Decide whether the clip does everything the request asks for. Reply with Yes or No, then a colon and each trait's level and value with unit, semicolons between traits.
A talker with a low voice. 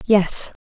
No: high, 195 Hz